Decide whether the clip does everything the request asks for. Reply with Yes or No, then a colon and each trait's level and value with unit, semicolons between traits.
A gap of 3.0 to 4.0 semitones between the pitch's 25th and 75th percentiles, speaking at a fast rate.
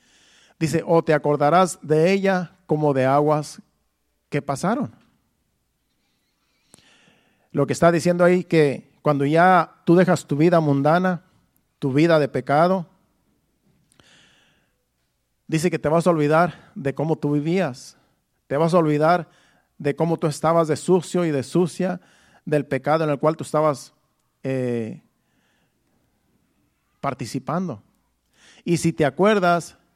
No: average, 3.4 semitones; average, 130 wpm